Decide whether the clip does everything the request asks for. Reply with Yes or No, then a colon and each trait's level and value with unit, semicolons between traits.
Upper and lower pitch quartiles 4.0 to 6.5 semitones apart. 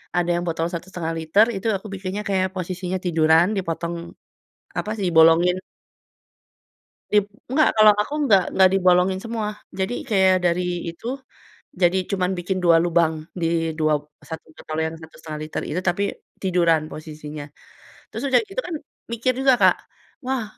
No: average, 2.9 semitones